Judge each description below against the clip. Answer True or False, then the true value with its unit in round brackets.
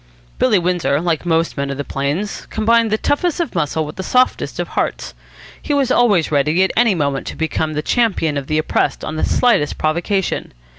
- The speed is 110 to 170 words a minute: False (200 wpm)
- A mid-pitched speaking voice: True (170 Hz)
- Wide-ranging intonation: True (6.4 semitones)